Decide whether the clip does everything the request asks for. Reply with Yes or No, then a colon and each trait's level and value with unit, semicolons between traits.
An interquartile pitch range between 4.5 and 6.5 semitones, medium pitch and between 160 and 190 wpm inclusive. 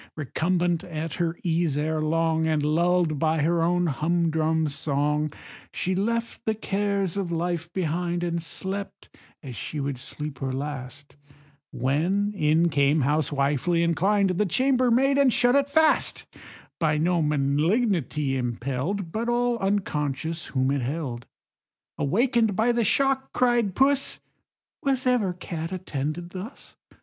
No: average, 5.1 semitones; medium, 170 Hz; slow, 135 wpm